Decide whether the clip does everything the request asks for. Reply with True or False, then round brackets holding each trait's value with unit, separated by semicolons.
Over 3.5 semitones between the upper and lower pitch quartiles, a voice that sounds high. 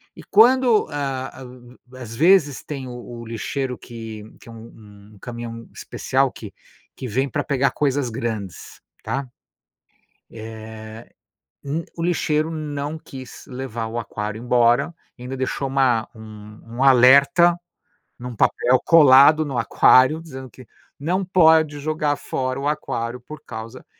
False (4.0 semitones; 130 Hz)